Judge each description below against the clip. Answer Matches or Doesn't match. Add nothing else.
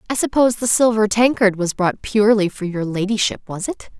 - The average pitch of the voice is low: Doesn't match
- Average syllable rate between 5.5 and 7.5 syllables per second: Matches